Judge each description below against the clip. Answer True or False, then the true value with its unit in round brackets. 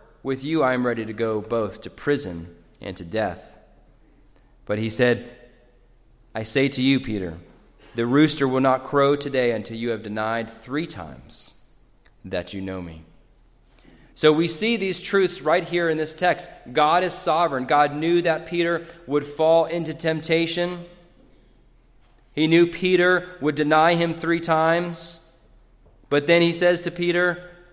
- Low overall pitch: False (145 Hz)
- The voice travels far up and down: True (6.5 semitones)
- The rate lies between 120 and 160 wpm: True (155 wpm)